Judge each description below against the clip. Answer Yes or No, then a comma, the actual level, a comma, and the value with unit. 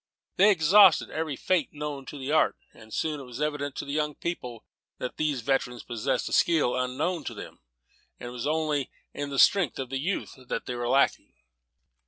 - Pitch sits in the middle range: Yes, medium, 145 Hz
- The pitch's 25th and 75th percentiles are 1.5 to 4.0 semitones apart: Yes, average, 3.6 semitones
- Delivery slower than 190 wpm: No, average, 195 wpm